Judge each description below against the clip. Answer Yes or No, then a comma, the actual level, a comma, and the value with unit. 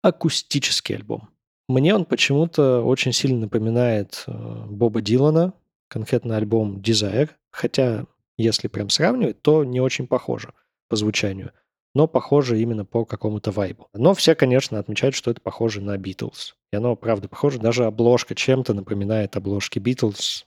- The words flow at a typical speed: Yes, average, 140 wpm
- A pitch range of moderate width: Yes, average, 3.8 semitones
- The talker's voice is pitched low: Yes, low, 120 Hz